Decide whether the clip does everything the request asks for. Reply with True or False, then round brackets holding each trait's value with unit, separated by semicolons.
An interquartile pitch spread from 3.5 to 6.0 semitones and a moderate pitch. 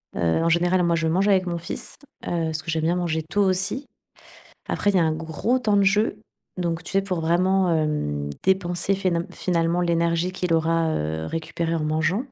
False (2.7 semitones; 170 Hz)